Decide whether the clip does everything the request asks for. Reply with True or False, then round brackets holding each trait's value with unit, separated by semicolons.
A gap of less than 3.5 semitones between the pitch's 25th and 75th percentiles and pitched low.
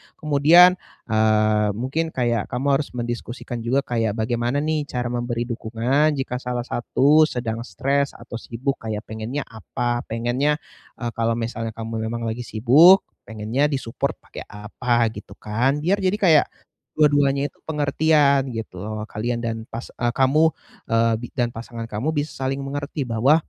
False (3.9 semitones; 120 Hz)